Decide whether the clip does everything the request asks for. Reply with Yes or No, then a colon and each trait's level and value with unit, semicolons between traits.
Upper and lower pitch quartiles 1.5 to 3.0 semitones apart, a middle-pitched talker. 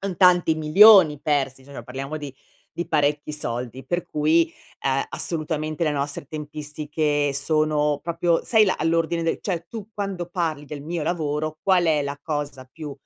Yes: narrow, 2.6 semitones; medium, 155 Hz